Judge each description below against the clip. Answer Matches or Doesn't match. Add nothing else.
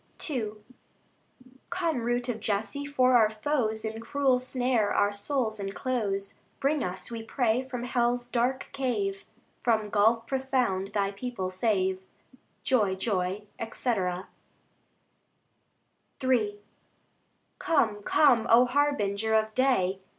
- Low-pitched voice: Doesn't match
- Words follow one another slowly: Matches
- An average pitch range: Matches